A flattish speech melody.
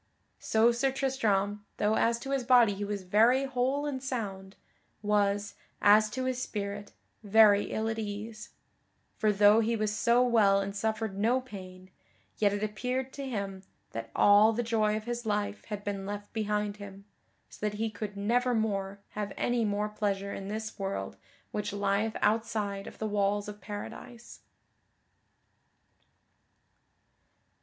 Yes: narrow, 2.3 semitones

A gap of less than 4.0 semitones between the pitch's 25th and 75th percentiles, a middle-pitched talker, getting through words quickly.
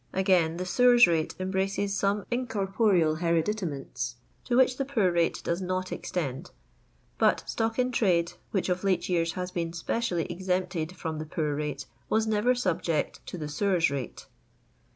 No: average, 3.6 semitones; medium, 180 Hz; average, 160 wpm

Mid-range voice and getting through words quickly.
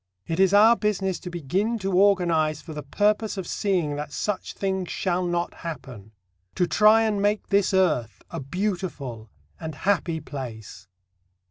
No: medium, 180 Hz; average, 155 wpm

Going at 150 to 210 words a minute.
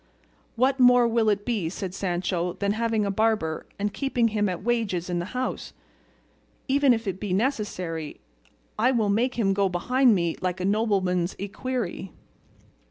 Yes: average, 165 wpm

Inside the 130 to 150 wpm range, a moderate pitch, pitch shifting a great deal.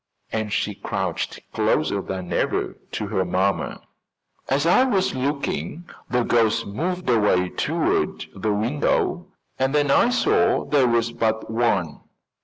No: slow, 135 wpm; low, 115 Hz; wide, 6.0 semitones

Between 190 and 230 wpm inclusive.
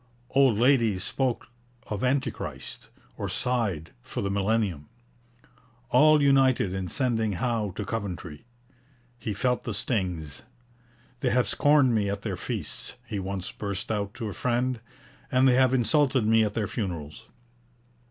No: average, 140 wpm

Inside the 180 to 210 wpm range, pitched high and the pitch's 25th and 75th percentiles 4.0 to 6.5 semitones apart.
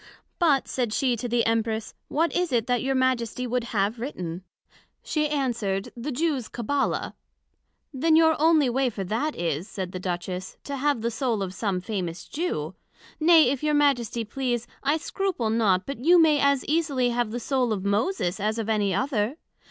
Yes: average, 185 wpm; high, 245 Hz; average, 5.1 semitones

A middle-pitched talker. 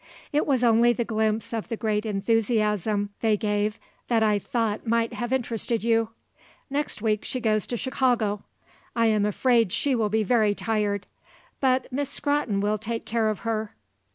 No: high, 225 Hz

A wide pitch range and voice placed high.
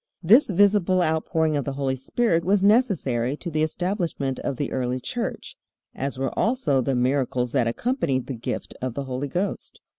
No: wide, 6.1 semitones; medium, 145 Hz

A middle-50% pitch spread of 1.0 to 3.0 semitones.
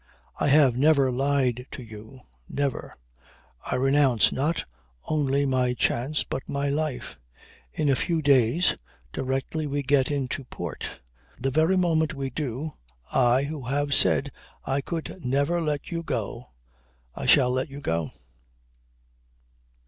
Yes: average, 2.7 semitones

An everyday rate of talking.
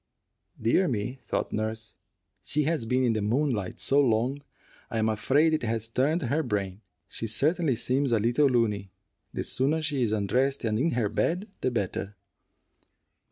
Yes: average, 165 wpm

